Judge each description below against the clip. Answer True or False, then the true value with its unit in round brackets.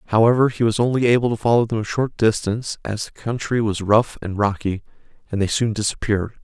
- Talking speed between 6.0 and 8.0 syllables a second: True (6.2 syllables/s)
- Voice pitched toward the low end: True (110 Hz)